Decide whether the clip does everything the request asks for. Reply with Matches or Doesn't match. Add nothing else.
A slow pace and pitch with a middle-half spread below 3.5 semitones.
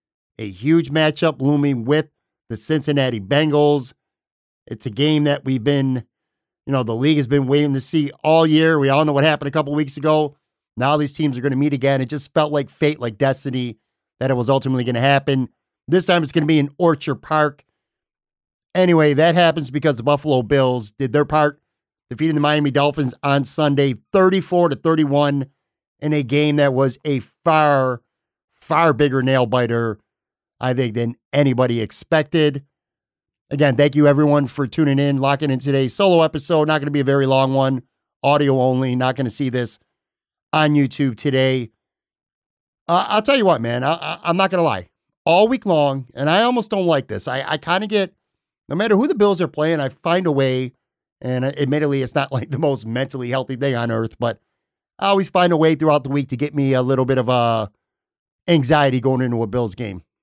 Doesn't match